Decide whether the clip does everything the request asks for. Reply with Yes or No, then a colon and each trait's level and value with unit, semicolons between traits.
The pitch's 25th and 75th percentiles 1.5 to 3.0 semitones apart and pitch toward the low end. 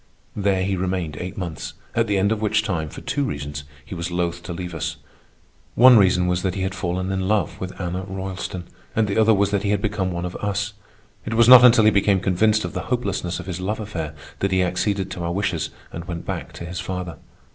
Yes: average, 2.7 semitones; very low, 95 Hz